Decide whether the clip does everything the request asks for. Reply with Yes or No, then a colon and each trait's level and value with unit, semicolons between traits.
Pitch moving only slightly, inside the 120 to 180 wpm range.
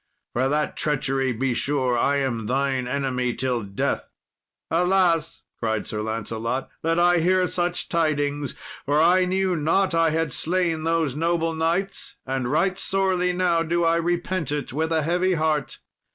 No: average, 4.5 semitones; average, 155 wpm